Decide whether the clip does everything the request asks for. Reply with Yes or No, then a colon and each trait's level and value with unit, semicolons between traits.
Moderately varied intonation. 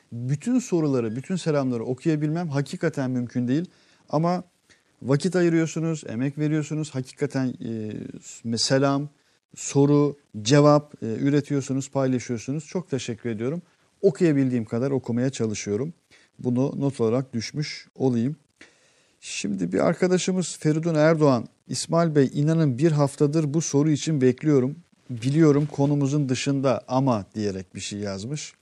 Yes: average, 3.7 semitones